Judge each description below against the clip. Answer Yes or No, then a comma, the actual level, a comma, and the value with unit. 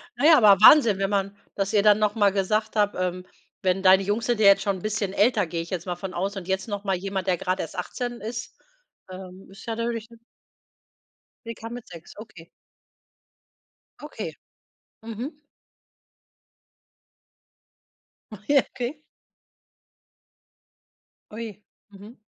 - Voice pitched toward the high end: Yes, high, 205 Hz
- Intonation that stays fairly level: No, average, 3.0 semitones